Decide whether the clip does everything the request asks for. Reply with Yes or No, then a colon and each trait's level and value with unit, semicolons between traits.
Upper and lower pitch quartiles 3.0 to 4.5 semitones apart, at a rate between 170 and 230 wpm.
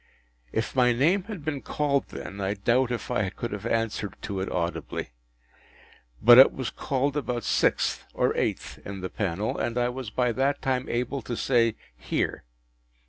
Yes: average, 4.1 semitones; average, 175 wpm